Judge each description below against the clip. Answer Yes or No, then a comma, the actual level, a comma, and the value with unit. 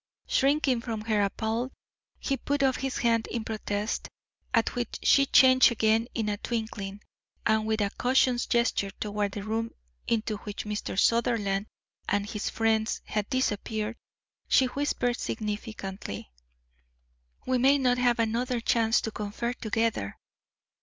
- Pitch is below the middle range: No, high, 225 Hz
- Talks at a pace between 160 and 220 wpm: No, average, 140 wpm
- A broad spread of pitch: No, average, 2.7 semitones